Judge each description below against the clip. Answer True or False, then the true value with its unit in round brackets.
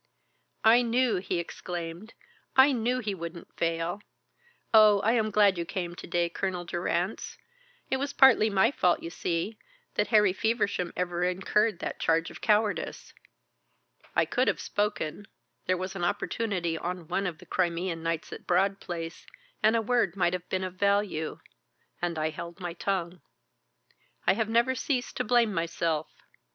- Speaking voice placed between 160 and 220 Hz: True (185 Hz)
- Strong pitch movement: False (4.0 semitones)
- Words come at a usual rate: True (165 wpm)